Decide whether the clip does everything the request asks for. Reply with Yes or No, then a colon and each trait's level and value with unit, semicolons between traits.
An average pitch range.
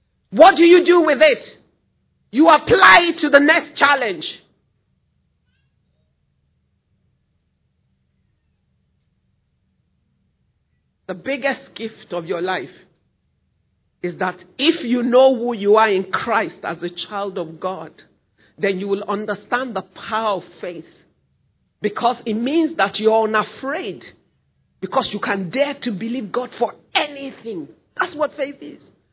No: wide, 7.4 semitones